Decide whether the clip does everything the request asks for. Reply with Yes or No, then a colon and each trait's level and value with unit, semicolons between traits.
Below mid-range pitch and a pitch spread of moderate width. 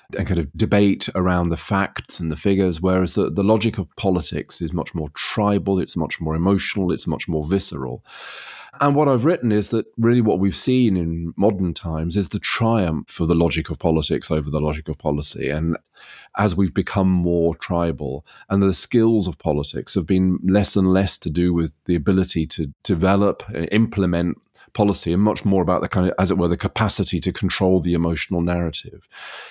Yes: very low, 90 Hz; average, 3.3 semitones